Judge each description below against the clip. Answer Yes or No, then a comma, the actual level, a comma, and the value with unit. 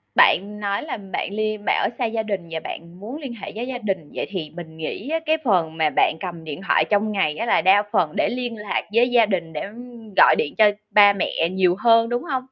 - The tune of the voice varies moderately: Yes, average, 4.9 semitones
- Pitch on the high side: Yes, high, 205 Hz